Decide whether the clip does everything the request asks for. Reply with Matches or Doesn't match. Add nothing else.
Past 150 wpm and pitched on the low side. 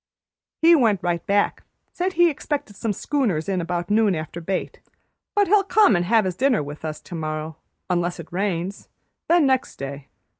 Doesn't match